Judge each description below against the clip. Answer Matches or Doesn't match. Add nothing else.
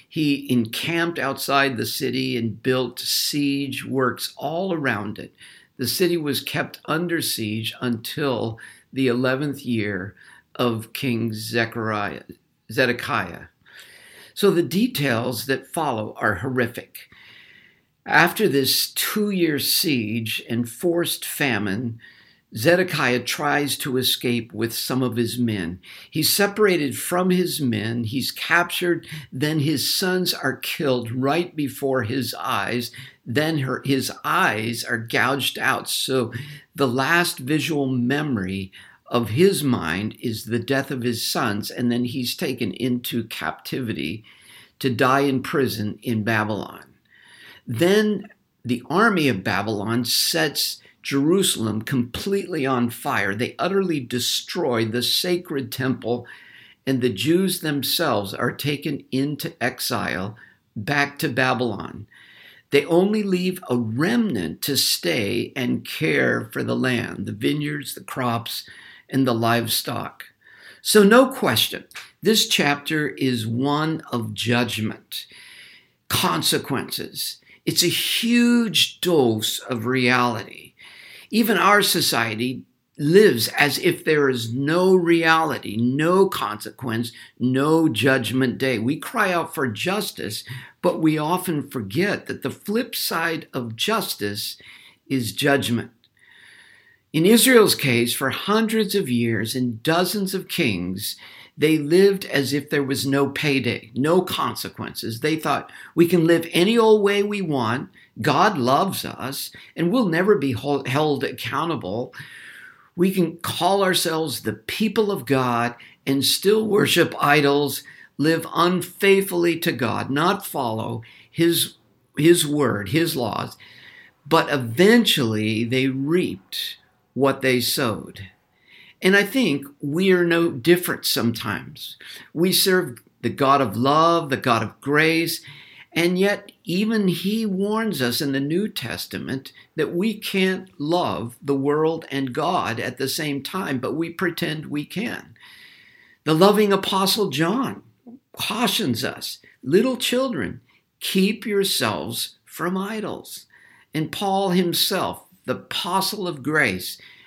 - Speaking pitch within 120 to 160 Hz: Matches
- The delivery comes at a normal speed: Doesn't match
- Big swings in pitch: Matches